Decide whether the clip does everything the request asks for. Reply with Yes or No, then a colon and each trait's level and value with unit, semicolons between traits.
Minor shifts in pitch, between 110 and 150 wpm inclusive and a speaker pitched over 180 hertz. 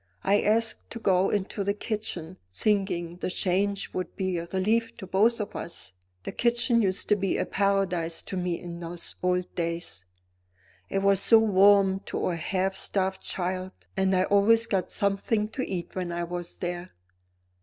No: narrow, 2.3 semitones; average, 175 wpm; high, 190 Hz